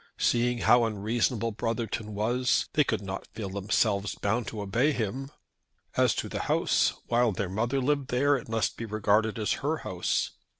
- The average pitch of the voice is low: Yes, low, 115 Hz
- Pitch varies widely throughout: No, average, 2.8 semitones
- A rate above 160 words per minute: Yes, average, 170 wpm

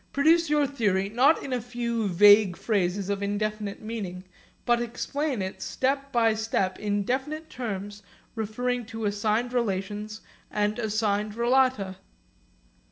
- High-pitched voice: Yes, high, 220 Hz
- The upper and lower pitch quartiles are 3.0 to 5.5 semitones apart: Yes, average, 3.4 semitones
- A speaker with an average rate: No, slow, 130 wpm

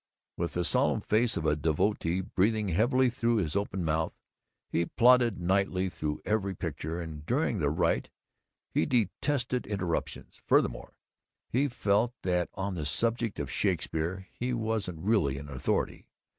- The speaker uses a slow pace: No, average, 145 wpm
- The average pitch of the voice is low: Yes, very low, 95 Hz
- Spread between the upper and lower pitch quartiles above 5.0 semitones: Yes, wide, 5.6 semitones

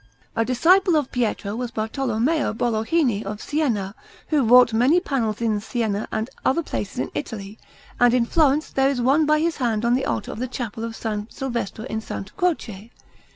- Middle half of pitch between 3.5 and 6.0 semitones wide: Yes, average, 4.1 semitones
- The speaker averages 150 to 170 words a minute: No, average, 185 wpm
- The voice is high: Yes, high, 240 Hz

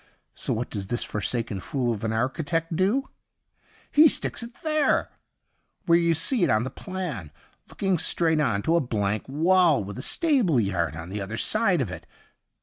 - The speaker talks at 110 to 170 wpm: No, average, 180 wpm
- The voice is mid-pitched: Yes, medium, 145 Hz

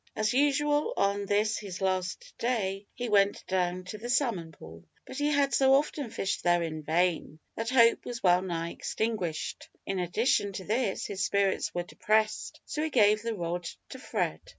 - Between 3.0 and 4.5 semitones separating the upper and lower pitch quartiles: No, average, 5.1 semitones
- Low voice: No, high, 205 Hz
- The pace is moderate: Yes, average, 180 wpm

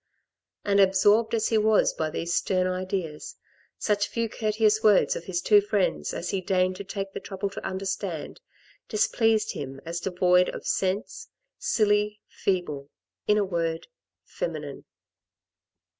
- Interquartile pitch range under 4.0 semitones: Yes, average, 2.7 semitones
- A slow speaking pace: No, average, 145 wpm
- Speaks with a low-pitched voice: No, high, 195 Hz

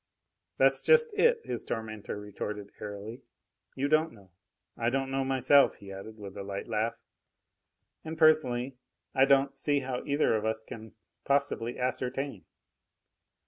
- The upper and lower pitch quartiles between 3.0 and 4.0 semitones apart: No, average, 4.5 semitones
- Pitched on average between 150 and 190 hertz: No, low, 125 Hz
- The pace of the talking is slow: No, average, 145 wpm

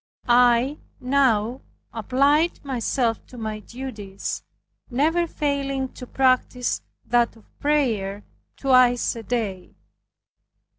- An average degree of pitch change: Yes, average, 3.2 semitones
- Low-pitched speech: No, very high, 250 Hz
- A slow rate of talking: Yes, slow, 95 wpm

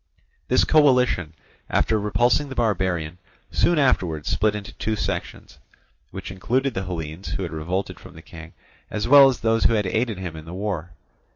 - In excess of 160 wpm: Yes, average, 175 wpm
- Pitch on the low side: Yes, low, 100 Hz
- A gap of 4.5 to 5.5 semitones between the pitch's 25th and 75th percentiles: Yes, average, 5.2 semitones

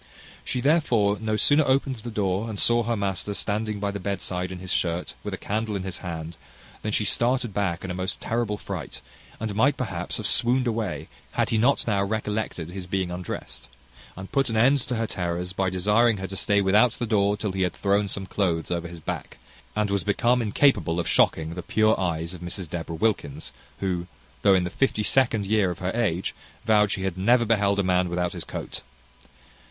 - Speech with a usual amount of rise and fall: Yes, average, 3.5 semitones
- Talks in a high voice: No, low, 100 Hz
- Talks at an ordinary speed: No, fast, 210 wpm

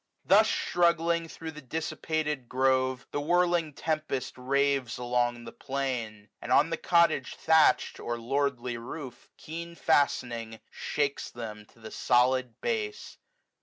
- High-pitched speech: No, low, 135 Hz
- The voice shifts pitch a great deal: No, average, 4.7 semitones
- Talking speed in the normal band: No, slow, 130 wpm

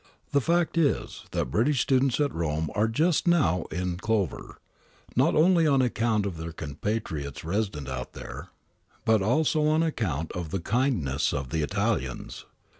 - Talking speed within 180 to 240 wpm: No, average, 155 wpm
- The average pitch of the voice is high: No, low, 105 Hz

